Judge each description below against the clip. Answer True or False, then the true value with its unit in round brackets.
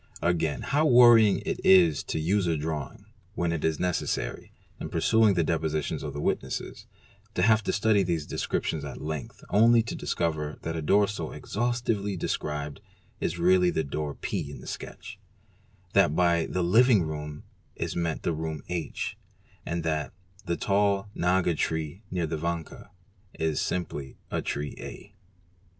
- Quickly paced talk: False (165 wpm)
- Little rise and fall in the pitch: False (4.3 semitones)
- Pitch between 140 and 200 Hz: False (85 Hz)